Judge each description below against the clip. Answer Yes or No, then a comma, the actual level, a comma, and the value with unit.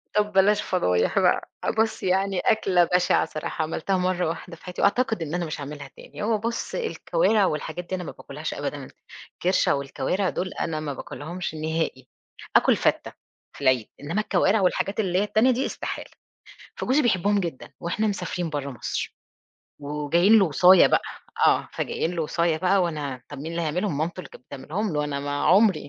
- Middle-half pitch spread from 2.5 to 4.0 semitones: No, average, 4.6 semitones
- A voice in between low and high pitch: Yes, medium, 175 Hz